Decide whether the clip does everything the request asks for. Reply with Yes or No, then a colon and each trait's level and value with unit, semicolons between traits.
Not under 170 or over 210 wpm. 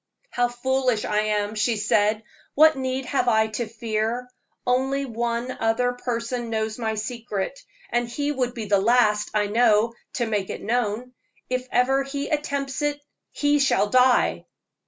No: average, 155 wpm